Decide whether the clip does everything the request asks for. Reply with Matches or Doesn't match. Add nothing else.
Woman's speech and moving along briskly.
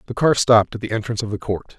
Doesn't match